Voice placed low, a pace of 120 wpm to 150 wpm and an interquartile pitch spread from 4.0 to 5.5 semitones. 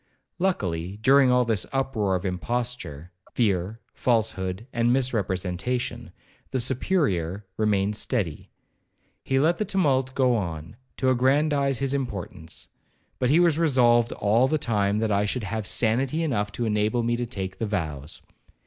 Yes: low, 115 Hz; average, 145 wpm; average, 4.9 semitones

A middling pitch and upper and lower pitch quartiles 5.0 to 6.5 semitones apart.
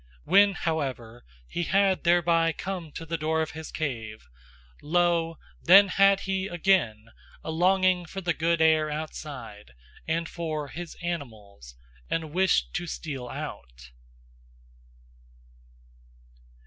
No: medium, 165 Hz; average, 3.6 semitones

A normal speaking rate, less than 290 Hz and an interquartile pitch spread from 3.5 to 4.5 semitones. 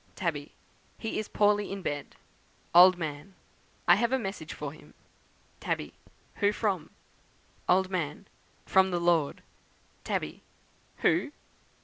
No: slow, 120 wpm; medium, 185 Hz; average, 4.2 semitones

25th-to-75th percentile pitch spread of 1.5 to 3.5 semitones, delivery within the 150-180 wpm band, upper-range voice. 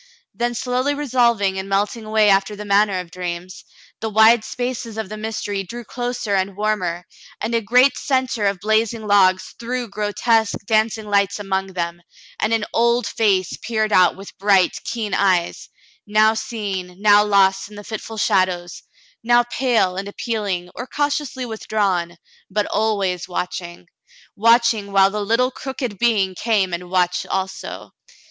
Yes: average, 3.2 semitones; average, 155 wpm; high, 210 Hz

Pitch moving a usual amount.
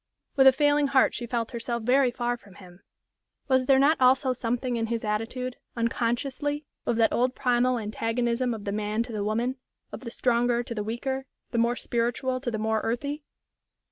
No: narrow, 2.2 semitones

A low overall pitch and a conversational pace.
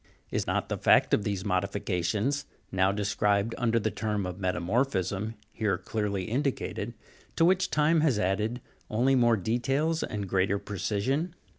Yes: low, 105 Hz; average, 150 wpm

